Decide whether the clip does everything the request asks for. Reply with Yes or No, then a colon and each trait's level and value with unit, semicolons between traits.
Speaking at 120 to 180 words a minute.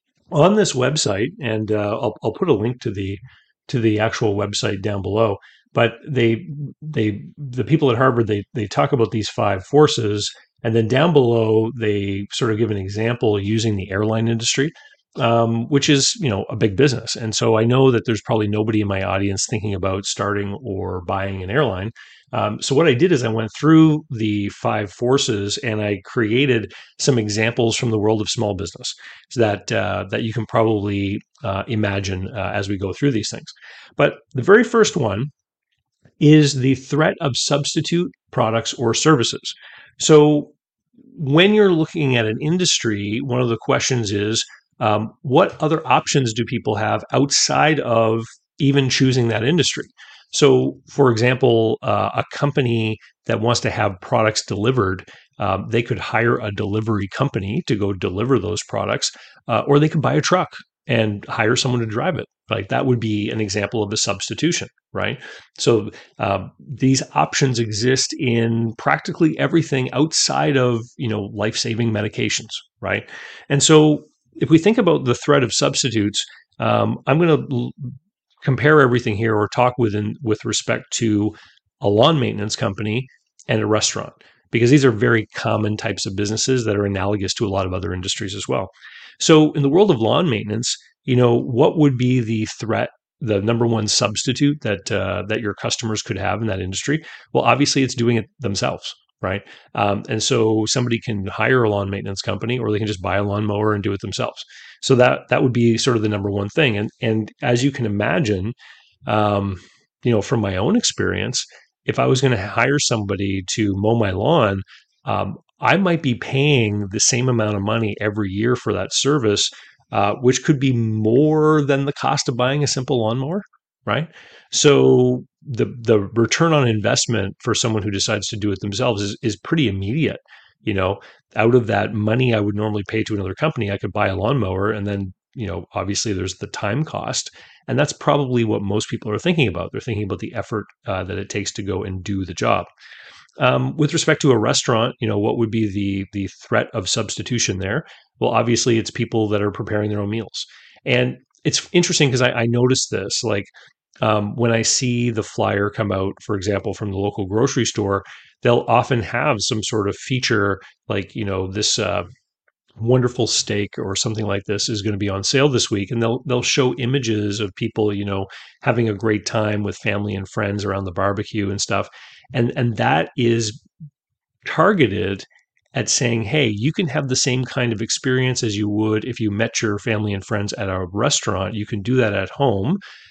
No: average, 190 wpm